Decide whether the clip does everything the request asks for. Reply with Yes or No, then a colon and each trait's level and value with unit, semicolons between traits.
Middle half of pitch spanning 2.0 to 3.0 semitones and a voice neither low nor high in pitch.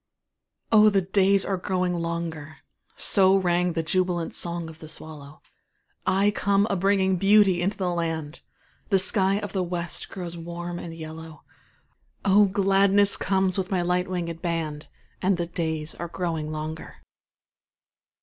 Yes: narrow, 2.6 semitones; medium, 180 Hz